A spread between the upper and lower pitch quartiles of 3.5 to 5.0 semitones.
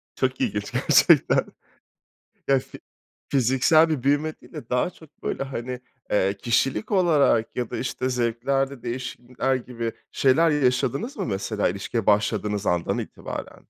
No: average, 3.1 semitones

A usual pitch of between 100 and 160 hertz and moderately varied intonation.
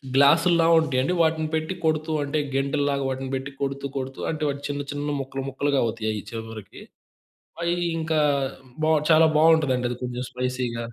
Yes: medium, 140 Hz; average, 3.4 semitones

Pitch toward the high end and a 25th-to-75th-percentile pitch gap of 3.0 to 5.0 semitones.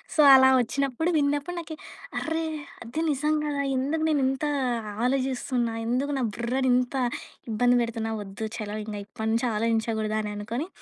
Yes: very high, 255 Hz; average, 3.9 semitones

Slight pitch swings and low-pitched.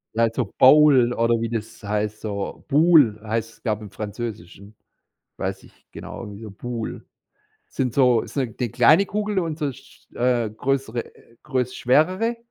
No: average, 4.0 semitones; low, 120 Hz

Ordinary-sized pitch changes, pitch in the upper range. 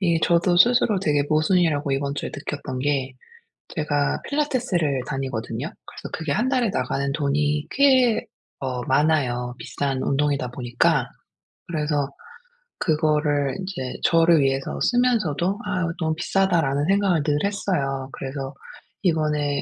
No: average, 4.6 semitones; medium, 150 Hz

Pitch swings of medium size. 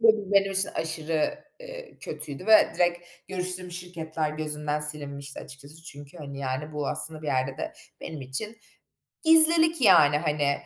Yes: average, 4.9 semitones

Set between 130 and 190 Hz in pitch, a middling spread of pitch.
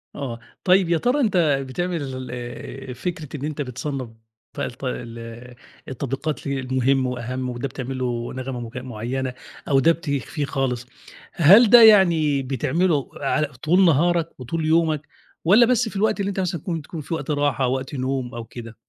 Yes: medium, 140 Hz; average, 4.6 semitones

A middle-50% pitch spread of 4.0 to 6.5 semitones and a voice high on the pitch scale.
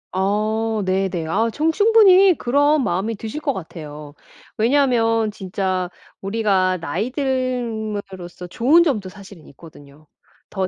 Yes: wide, 5.4 semitones; high, 215 Hz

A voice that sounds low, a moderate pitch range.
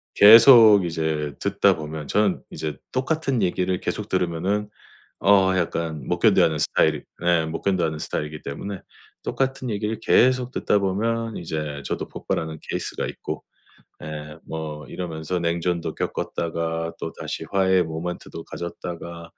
Yes: very low, 85 Hz; average, 4.3 semitones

